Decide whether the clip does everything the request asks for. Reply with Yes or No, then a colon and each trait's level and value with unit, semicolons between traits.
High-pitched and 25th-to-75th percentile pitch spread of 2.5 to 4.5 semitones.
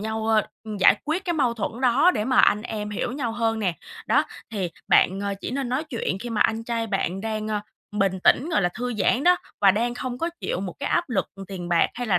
Yes: high, 225 Hz; average, 3.7 semitones